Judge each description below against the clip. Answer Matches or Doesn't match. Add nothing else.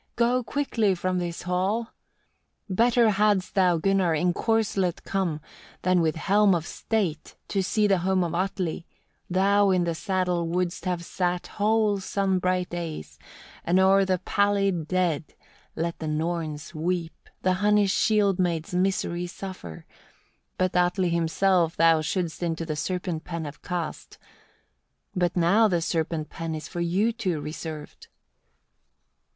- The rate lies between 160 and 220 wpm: Doesn't match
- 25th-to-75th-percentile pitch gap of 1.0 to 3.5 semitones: Matches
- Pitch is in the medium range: Matches